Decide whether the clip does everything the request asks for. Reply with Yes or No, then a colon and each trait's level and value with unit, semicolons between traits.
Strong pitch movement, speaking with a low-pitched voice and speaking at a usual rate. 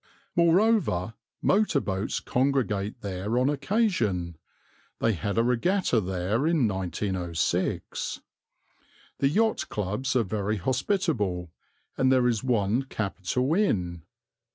No: wide, 6.4 semitones; low, 115 Hz; slow, 105 wpm